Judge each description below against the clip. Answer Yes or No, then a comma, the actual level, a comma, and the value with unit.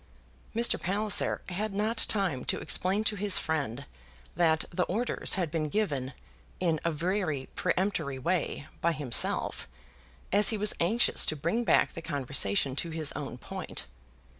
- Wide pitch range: Yes, wide, 5.9 semitones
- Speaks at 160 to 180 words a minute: No, average, 150 wpm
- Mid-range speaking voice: Yes, medium, 170 Hz